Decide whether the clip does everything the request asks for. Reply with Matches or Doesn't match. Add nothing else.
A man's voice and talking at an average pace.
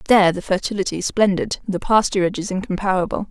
Doesn't match